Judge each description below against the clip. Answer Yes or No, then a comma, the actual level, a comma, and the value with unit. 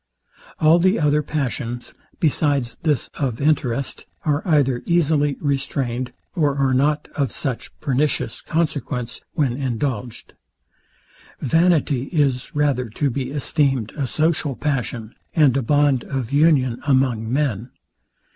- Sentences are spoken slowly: Yes, slow, 120 wpm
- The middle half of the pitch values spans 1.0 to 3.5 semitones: Yes, average, 3.0 semitones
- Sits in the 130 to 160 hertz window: Yes, medium, 140 Hz